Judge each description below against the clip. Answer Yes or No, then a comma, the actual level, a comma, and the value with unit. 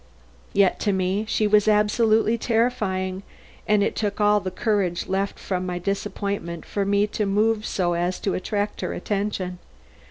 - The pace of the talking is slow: No, average, 160 wpm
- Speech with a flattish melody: Yes, narrow, 2.1 semitones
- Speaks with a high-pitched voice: Yes, high, 200 Hz